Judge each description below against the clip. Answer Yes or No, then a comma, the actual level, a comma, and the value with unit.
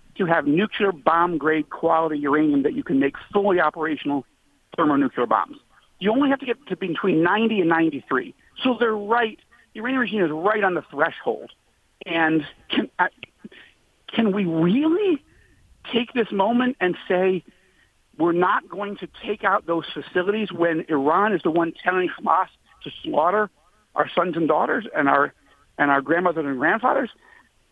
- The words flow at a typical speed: Yes, average, 160 wpm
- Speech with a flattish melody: No, average, 4.9 semitones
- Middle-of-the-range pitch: Yes, medium, 180 Hz